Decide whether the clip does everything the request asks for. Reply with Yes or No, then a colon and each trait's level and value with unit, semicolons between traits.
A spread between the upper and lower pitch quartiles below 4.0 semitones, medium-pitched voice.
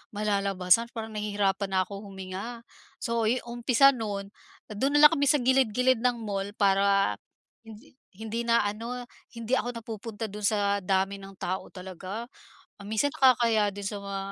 No: average, 3.1 semitones; high, 215 Hz